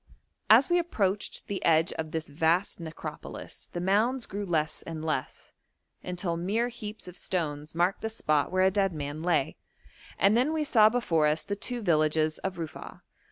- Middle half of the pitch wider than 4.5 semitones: Yes, average, 5.0 semitones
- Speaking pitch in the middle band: Yes, medium, 180 Hz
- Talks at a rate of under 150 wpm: No, average, 175 wpm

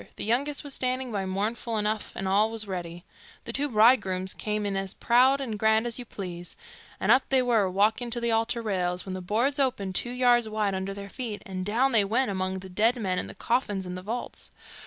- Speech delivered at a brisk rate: Yes, fast, 225 wpm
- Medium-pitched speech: No, high, 215 Hz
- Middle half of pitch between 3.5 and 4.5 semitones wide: Yes, average, 4.0 semitones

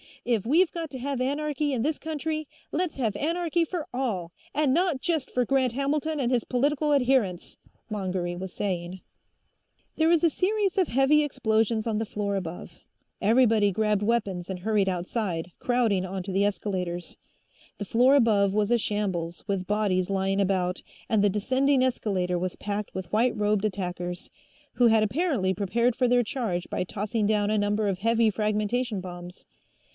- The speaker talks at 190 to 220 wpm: No, average, 170 wpm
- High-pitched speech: Yes, high, 215 Hz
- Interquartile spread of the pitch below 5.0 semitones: No, wide, 5.5 semitones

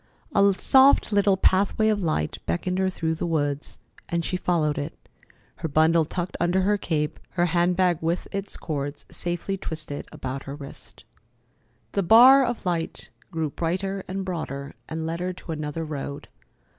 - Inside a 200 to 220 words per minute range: No, average, 165 wpm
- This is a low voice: No, medium, 170 Hz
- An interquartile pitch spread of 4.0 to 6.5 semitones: No, average, 3.5 semitones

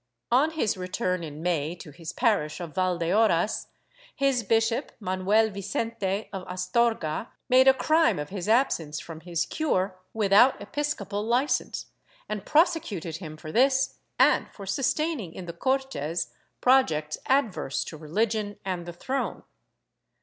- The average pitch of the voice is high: Yes, high, 200 Hz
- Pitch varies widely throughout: Yes, wide, 6.2 semitones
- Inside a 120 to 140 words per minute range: Yes, slow, 135 wpm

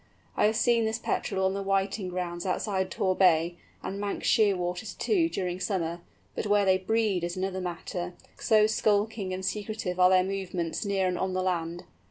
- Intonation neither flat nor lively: No, narrow, 2.3 semitones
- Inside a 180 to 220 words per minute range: Yes, average, 185 wpm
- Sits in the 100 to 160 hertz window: No, high, 190 Hz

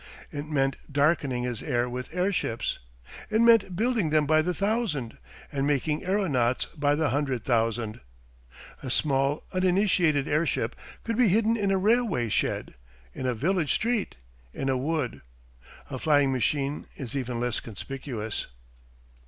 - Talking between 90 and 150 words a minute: Yes, average, 145 wpm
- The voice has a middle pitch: Yes, medium, 145 Hz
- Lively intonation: Yes, wide, 6.4 semitones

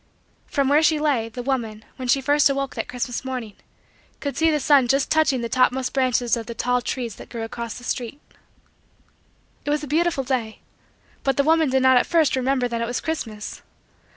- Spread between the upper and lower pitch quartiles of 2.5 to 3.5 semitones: Yes, average, 3.0 semitones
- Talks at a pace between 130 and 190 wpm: No, fast, 205 wpm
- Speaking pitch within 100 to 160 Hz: No, very high, 260 Hz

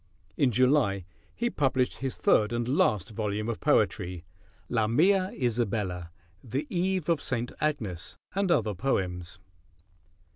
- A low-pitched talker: Yes, low, 120 Hz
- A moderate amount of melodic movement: No, wide, 5.9 semitones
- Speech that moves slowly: Yes, slow, 120 wpm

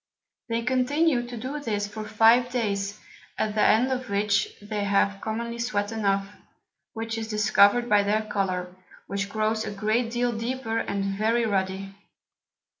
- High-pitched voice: Yes, high, 215 Hz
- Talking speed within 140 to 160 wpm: Yes, average, 155 wpm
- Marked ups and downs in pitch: No, narrow, 2.6 semitones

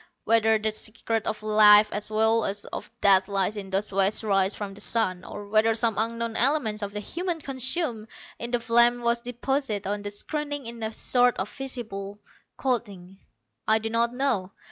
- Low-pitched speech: No, high, 220 Hz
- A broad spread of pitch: No, average, 2.7 semitones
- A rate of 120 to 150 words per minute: No, average, 185 wpm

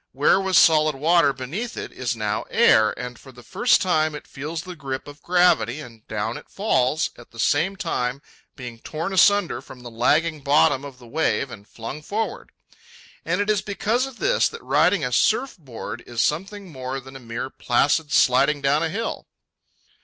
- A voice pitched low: No, medium, 145 Hz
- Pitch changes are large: Yes, wide, 6.0 semitones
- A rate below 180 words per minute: No, average, 190 wpm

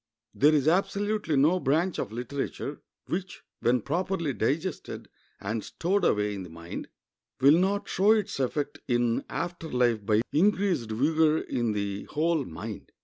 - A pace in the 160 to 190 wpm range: No, average, 145 wpm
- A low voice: No, medium, 145 Hz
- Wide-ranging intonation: Yes, wide, 7.2 semitones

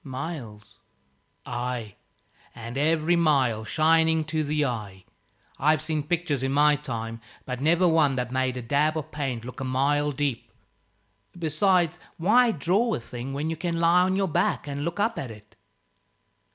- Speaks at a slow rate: No, average, 165 wpm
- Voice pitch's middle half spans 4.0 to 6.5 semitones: Yes, average, 4.4 semitones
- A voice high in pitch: No, medium, 145 Hz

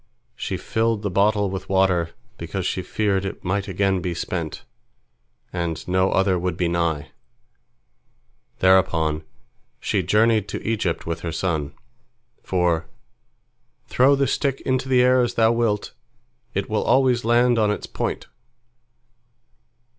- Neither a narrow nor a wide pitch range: Yes, average, 4.3 semitones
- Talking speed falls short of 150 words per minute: Yes, slow, 135 wpm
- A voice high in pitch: No, very low, 95 Hz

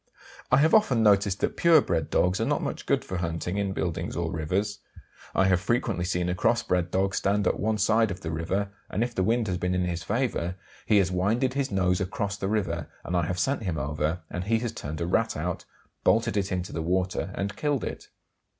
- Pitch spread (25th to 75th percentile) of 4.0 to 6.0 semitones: No, average, 3.4 semitones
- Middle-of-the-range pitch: No, very low, 95 Hz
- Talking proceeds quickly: Yes, fast, 230 wpm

